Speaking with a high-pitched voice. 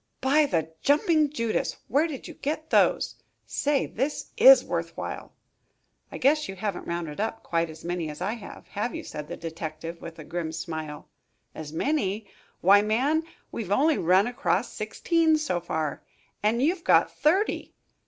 Yes: high, 210 Hz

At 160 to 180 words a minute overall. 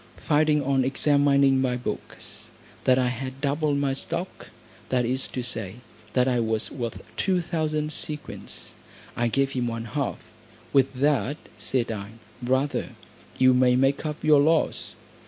No: average, 150 wpm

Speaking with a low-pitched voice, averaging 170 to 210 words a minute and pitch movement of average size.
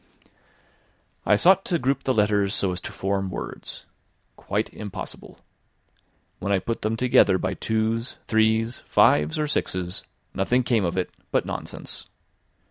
No: low, 110 Hz; average, 140 wpm; average, 3.8 semitones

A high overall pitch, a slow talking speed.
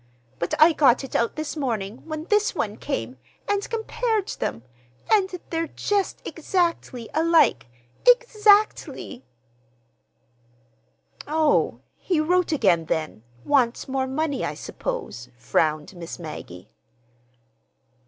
Yes: very high, 300 Hz; slow, 105 wpm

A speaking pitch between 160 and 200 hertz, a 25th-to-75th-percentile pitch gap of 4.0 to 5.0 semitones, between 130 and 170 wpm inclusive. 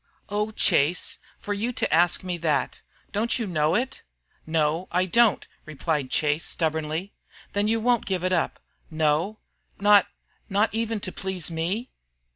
Yes: medium, 185 Hz; average, 4.7 semitones; average, 150 wpm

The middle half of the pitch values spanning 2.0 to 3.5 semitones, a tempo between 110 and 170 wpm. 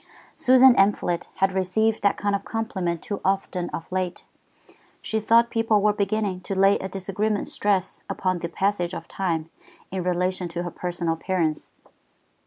Yes: narrow, 2.6 semitones; average, 160 wpm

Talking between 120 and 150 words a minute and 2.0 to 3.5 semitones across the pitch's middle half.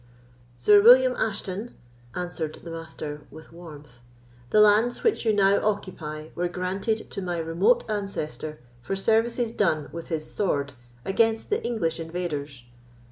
No: slow, 135 wpm; wide, 5.4 semitones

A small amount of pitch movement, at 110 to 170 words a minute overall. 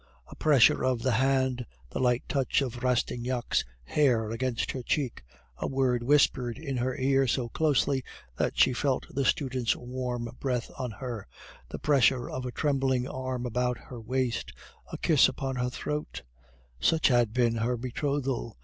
Yes: narrow, 1.8 semitones; average, 160 wpm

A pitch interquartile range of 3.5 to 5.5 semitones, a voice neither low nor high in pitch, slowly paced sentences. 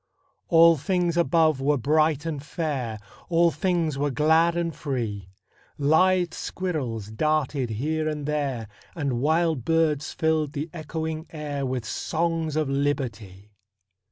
No: average, 3.1 semitones; medium, 155 Hz; slow, 125 wpm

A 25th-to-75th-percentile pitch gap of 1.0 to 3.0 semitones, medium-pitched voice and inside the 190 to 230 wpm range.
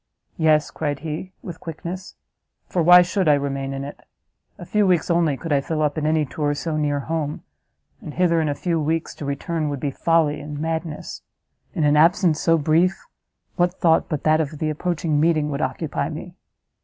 Yes: narrow, 2.4 semitones; medium, 155 Hz; average, 195 wpm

